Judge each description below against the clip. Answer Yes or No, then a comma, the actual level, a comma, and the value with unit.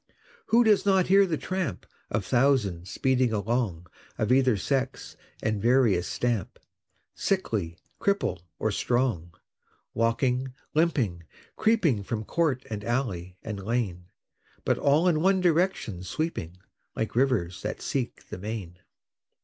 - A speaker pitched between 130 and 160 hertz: No, low, 120 Hz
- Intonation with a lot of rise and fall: Yes, wide, 6.9 semitones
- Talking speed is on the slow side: Yes, slow, 125 wpm